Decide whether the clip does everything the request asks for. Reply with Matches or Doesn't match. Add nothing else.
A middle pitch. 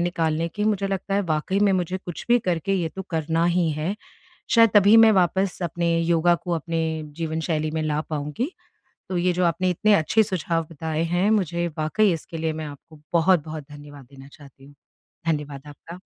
Matches